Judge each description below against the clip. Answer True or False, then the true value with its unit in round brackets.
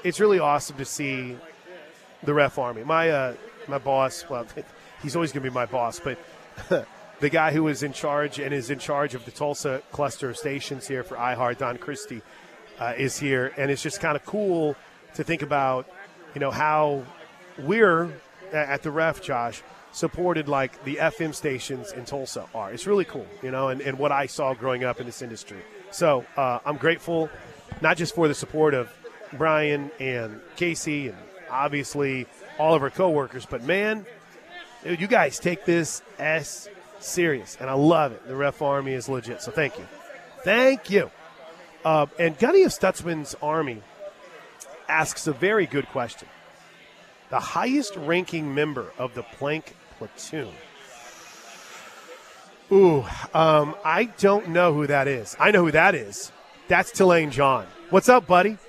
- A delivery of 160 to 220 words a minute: True (170 wpm)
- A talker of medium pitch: True (150 Hz)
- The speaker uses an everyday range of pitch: True (3.9 semitones)